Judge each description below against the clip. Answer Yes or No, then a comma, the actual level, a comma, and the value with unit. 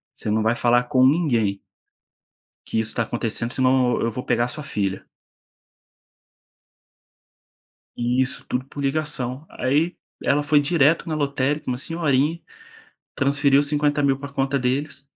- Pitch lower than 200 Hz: Yes, low, 135 Hz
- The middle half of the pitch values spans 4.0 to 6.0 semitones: No, average, 3.0 semitones